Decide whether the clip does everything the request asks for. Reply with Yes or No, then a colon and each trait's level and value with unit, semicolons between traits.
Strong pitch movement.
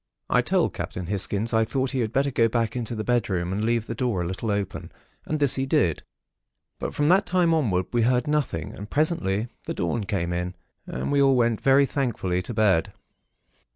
Yes: wide, 5.7 semitones